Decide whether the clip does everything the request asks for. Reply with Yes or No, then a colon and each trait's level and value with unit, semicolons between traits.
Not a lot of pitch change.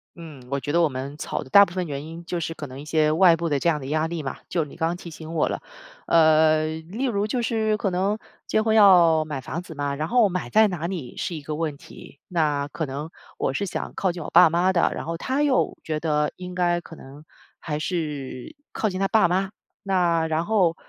No: average, 3.3 semitones